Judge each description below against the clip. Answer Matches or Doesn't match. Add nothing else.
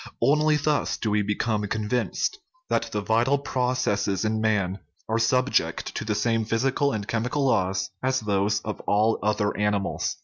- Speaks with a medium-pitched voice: Doesn't match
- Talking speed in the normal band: Matches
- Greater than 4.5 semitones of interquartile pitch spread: Doesn't match